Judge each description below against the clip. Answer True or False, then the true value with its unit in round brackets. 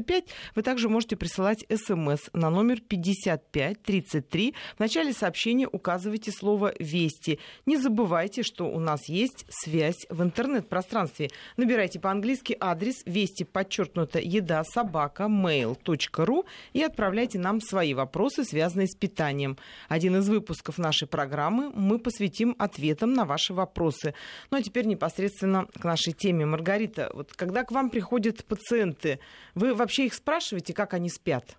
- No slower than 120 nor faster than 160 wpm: True (135 wpm)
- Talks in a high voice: True (195 Hz)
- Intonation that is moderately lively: False (5.7 semitones)